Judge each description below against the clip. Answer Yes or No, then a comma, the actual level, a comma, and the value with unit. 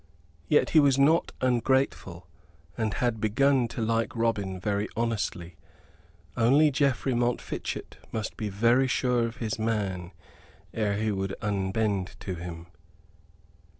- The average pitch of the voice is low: Yes, low, 110 Hz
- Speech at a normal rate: No, slow, 125 wpm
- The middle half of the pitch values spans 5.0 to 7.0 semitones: No, average, 3.6 semitones